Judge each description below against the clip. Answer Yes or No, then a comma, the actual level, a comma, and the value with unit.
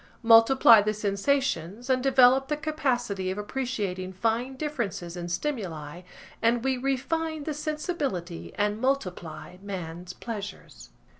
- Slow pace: Yes, slow, 120 wpm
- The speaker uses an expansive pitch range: Yes, wide, 6.3 semitones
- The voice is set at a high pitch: Yes, high, 230 Hz